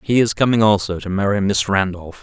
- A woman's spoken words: No, male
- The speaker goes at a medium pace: No, fast, 215 wpm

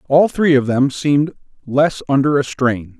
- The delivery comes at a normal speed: Yes, average, 180 wpm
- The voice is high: No, medium, 140 Hz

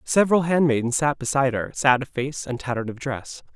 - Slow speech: No, fast, 205 wpm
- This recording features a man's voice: Yes, male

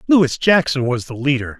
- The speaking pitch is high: No, medium, 140 Hz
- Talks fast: No, average, 190 wpm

